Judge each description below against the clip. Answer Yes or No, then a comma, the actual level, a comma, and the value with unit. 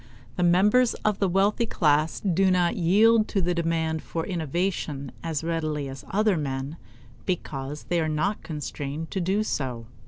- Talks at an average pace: Yes, average, 160 wpm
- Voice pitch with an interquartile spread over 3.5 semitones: Yes, average, 4.3 semitones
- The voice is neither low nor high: Yes, medium, 165 Hz